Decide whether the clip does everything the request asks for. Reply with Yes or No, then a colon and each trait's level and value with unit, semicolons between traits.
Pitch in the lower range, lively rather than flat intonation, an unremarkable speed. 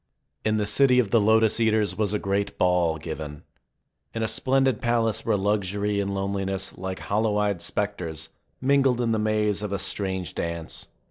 No: low, 105 Hz; average, 2.7 semitones; average, 175 wpm